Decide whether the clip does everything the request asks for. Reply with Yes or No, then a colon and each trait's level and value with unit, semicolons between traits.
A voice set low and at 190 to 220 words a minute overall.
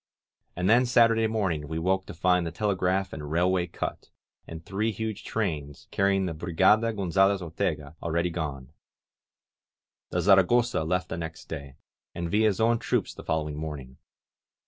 No: very low, 90 Hz; average, 150 wpm